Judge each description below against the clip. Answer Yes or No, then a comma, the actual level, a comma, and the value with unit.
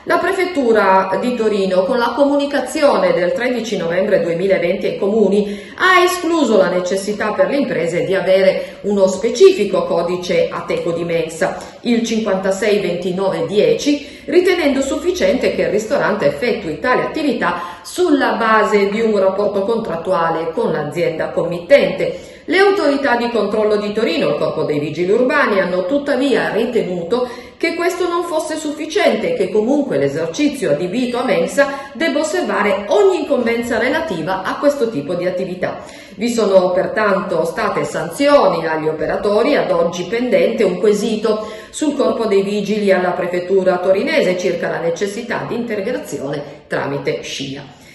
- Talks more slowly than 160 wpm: Yes, average, 140 wpm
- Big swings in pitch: Yes, wide, 6.9 semitones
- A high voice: Yes, high, 215 Hz